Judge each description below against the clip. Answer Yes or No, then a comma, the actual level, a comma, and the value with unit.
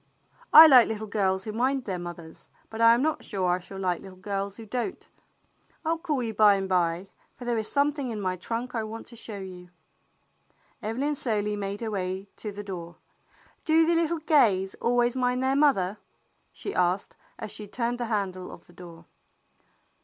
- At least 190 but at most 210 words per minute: Yes, average, 200 wpm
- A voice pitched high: Yes, high, 215 Hz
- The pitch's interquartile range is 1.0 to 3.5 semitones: No, average, 4.7 semitones